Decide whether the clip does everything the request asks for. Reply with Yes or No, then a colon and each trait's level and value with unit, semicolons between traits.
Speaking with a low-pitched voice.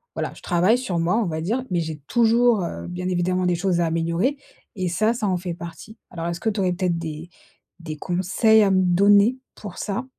No: medium, 180 Hz